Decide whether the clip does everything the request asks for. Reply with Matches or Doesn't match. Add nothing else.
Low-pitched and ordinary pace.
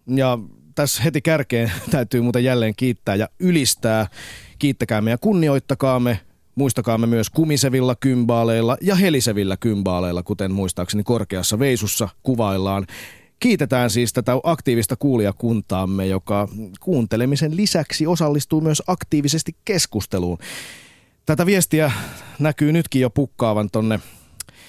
Matches